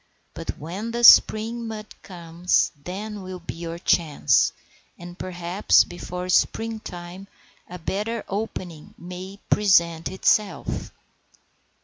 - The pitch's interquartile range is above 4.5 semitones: No, average, 3.4 semitones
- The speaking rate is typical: No, slow, 110 wpm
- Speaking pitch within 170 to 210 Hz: Yes, medium, 185 Hz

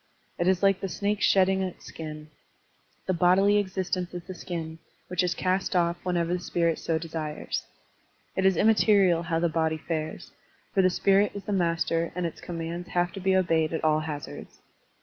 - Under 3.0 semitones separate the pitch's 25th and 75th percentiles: Yes, narrow, 2.5 semitones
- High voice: No, medium, 175 Hz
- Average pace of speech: Yes, average, 185 wpm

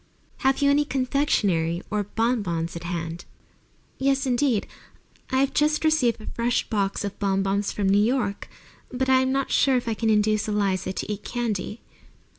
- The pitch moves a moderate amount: Yes, average, 4.9 semitones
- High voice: Yes, high, 220 Hz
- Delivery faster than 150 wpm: Yes, average, 170 wpm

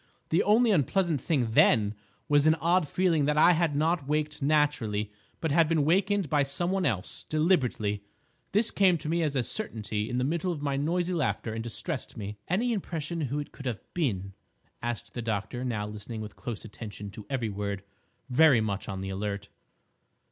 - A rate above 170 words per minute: Yes, average, 185 wpm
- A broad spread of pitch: Yes, wide, 7.3 semitones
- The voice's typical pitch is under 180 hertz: Yes, medium, 140 Hz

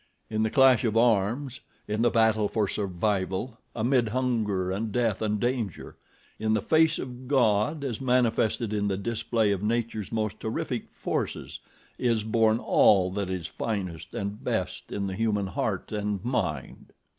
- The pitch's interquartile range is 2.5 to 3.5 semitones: Yes, average, 2.9 semitones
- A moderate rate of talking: Yes, average, 155 wpm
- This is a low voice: Yes, low, 110 Hz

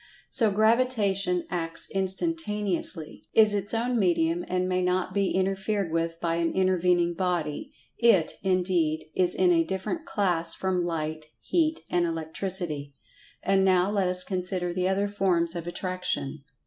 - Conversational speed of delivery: Yes, average, 145 wpm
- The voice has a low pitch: No, medium, 185 Hz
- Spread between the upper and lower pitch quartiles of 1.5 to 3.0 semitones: Yes, narrow, 2.6 semitones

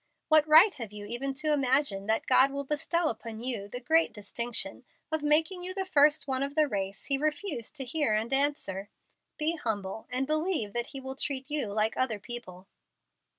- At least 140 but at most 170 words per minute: No, average, 195 wpm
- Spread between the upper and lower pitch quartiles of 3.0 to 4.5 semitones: No, wide, 5.5 semitones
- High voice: Yes, very high, 270 Hz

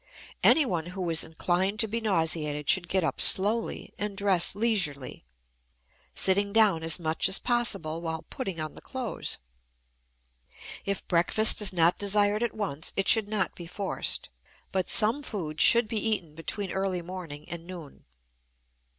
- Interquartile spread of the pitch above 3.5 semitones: Yes, average, 4.4 semitones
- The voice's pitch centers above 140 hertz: Yes, high, 190 Hz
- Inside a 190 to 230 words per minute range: No, average, 150 wpm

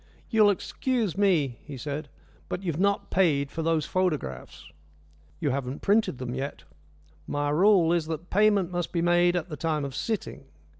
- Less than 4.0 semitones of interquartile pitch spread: No, average, 4.9 semitones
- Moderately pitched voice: Yes, medium, 165 Hz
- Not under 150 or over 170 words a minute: Yes, average, 165 wpm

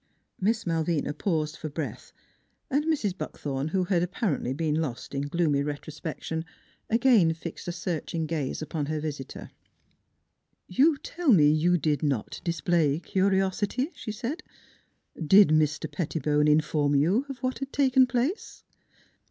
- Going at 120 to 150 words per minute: No, average, 160 wpm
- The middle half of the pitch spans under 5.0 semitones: No, wide, 5.5 semitones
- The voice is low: No, medium, 165 Hz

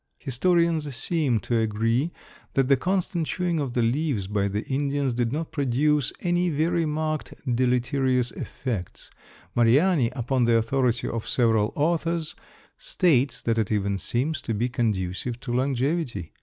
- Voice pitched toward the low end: Yes, low, 130 Hz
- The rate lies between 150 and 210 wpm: No, average, 140 wpm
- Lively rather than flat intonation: No, average, 4.9 semitones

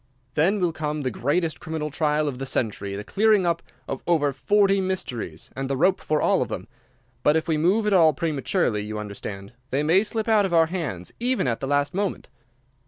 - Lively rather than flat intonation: Yes, wide, 5.7 semitones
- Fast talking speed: Yes, fast, 210 wpm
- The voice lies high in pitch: No, medium, 155 Hz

